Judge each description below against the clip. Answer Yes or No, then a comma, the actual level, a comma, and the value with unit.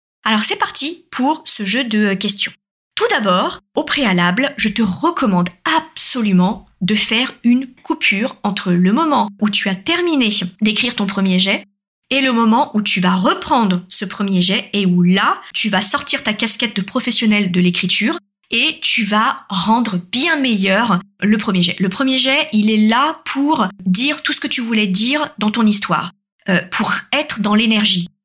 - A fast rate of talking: No, average, 175 wpm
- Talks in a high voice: Yes, high, 215 Hz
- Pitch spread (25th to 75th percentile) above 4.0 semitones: Yes, average, 4.9 semitones